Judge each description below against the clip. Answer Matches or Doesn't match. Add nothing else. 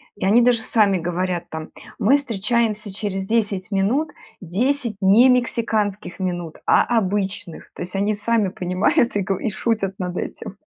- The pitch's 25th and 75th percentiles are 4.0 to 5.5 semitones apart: Doesn't match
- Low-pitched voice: Doesn't match